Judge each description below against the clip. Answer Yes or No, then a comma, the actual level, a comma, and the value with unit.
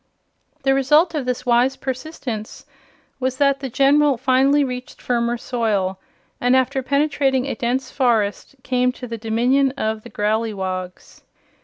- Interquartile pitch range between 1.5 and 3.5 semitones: Yes, average, 2.8 semitones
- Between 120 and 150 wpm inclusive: Yes, average, 140 wpm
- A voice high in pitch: Yes, very high, 255 Hz